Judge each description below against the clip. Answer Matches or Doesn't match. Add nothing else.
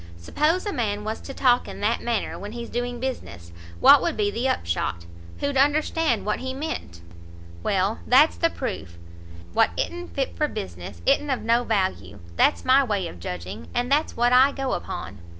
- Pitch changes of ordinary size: Doesn't match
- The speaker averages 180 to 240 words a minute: Matches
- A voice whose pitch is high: Matches